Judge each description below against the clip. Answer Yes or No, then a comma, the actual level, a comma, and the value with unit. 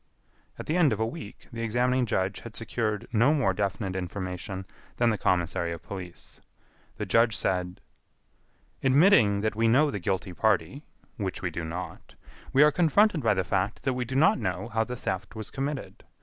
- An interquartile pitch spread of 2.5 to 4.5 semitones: No, average, 5.2 semitones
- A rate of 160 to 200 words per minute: Yes, average, 185 wpm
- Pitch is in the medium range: No, low, 110 Hz